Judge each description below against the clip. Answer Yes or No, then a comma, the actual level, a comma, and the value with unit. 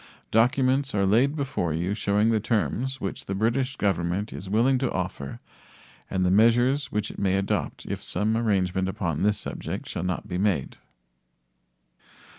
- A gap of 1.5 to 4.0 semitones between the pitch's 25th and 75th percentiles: No, average, 4.4 semitones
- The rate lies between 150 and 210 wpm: Yes, average, 160 wpm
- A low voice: Yes, low, 105 Hz